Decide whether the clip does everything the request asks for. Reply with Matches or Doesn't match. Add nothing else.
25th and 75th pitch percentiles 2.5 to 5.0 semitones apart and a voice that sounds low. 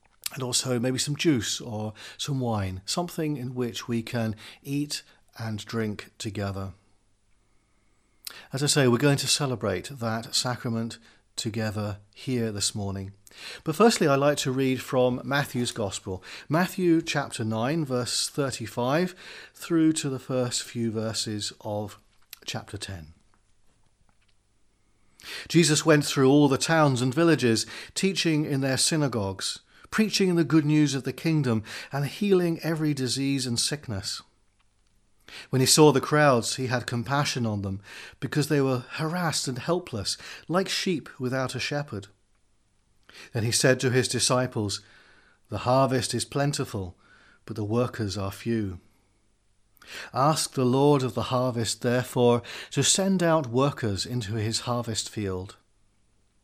Doesn't match